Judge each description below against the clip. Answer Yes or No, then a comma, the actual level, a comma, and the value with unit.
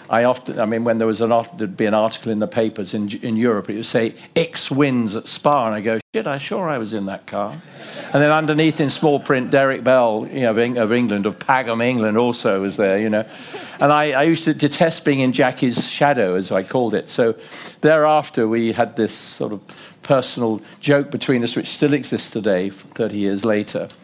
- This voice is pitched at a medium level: No, low, 120 Hz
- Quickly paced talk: Yes, fast, 220 wpm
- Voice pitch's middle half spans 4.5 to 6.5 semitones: Yes, average, 4.8 semitones